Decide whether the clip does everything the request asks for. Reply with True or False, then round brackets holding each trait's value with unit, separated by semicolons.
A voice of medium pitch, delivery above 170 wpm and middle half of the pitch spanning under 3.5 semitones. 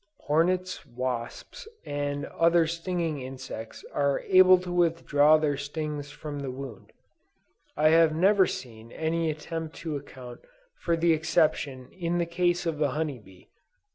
False (155 Hz; 140 wpm; 3.1 semitones)